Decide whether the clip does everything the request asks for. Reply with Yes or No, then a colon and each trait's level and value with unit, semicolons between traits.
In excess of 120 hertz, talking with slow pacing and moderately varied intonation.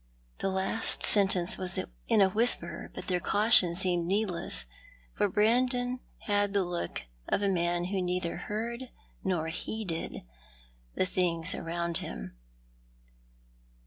Yes: high, 190 Hz; slow, 125 wpm; average, 3.3 semitones